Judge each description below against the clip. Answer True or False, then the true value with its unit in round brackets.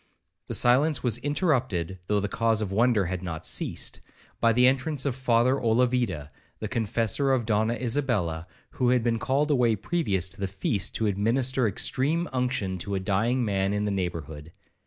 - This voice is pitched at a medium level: False (115 Hz)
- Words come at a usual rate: True (175 wpm)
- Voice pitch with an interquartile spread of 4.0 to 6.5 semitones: True (4.7 semitones)